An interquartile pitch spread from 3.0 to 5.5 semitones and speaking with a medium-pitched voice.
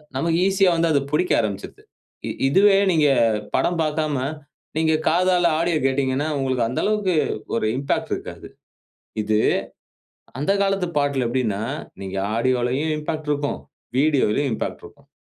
Yes: average, 4.4 semitones; medium, 150 Hz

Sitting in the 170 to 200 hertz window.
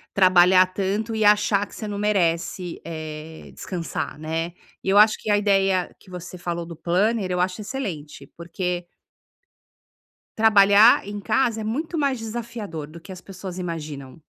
Yes: high, 190 Hz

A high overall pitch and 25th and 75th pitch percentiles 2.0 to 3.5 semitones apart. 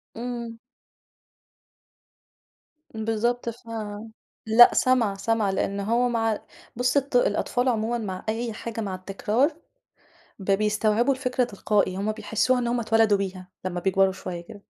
Yes: high, 225 Hz; average, 3.2 semitones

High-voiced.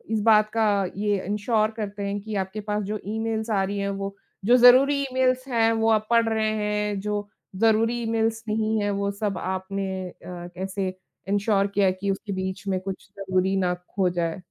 Yes: high, 205 Hz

